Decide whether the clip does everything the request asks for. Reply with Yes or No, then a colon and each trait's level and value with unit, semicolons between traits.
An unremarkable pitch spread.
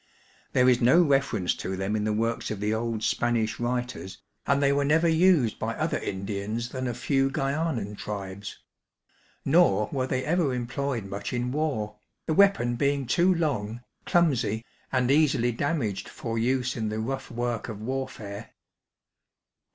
Yes: average, 4.3 semitones